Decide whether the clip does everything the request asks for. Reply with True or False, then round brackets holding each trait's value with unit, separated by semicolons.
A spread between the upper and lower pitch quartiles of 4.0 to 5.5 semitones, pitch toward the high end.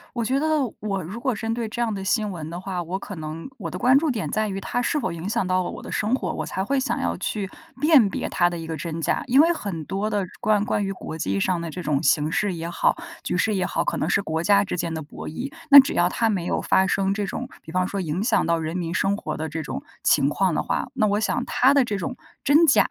True (5.0 semitones; 195 Hz)